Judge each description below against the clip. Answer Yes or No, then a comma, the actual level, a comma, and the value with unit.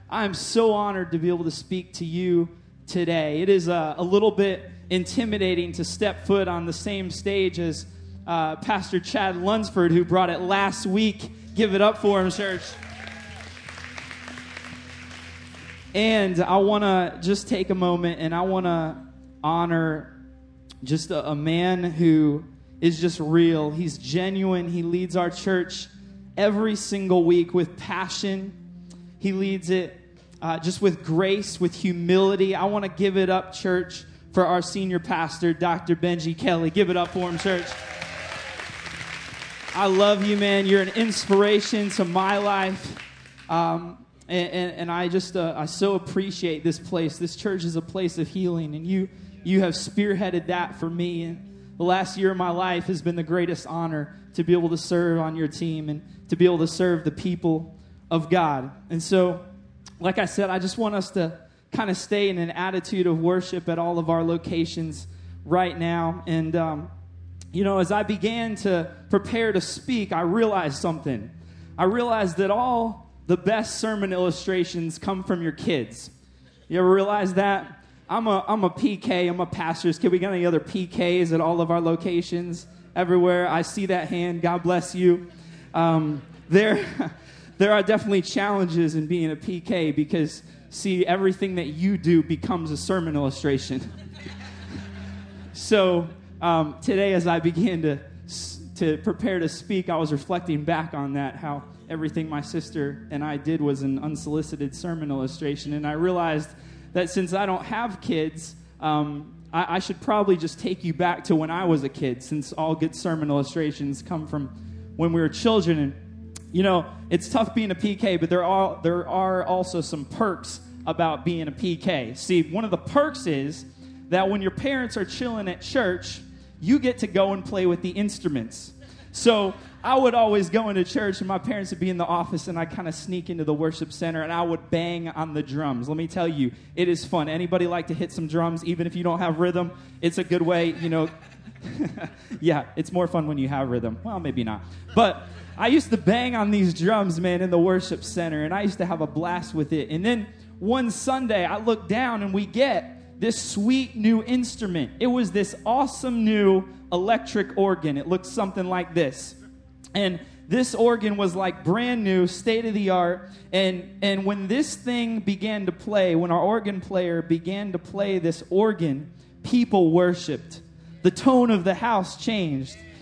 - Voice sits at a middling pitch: Yes, medium, 175 Hz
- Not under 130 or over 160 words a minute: No, average, 185 wpm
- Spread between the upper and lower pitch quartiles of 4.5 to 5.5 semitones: No, average, 3.3 semitones